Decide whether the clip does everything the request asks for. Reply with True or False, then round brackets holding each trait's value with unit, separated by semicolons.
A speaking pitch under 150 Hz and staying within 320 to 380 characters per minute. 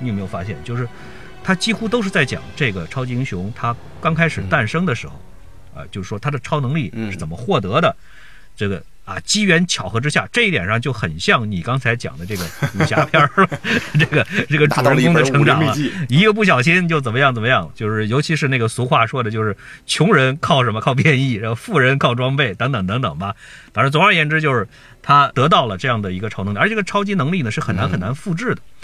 True (135 Hz; 345 characters per minute)